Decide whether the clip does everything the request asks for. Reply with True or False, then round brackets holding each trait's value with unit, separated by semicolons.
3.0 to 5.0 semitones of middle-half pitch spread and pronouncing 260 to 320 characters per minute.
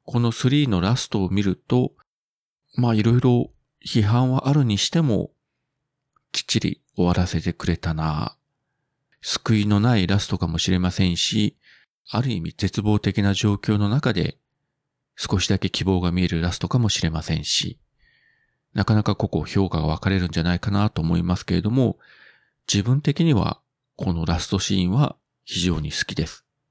True (4.1 semitones; 310 characters per minute)